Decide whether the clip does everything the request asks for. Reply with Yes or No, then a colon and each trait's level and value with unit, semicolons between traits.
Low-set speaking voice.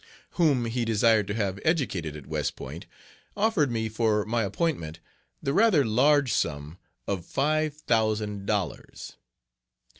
Yes: low, 115 Hz